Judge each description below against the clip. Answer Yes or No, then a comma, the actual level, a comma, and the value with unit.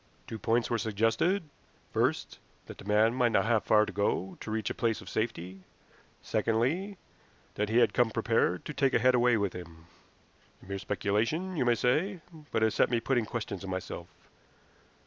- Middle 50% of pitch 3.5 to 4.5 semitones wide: No, average, 3.1 semitones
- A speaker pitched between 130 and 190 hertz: No, low, 115 Hz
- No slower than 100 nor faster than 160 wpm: No, average, 185 wpm